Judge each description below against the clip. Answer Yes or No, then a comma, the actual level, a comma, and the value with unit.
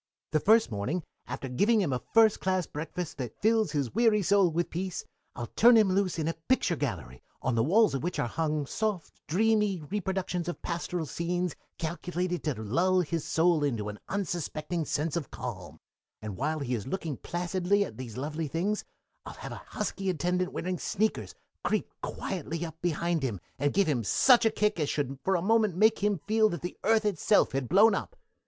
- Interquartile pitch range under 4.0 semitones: No, average, 5.3 semitones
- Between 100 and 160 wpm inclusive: No, average, 195 wpm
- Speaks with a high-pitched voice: No, medium, 175 Hz